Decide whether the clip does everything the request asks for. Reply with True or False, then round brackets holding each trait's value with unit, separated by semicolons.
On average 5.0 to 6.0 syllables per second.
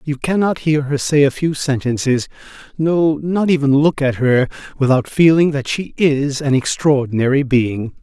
False (4.6 syllables/s)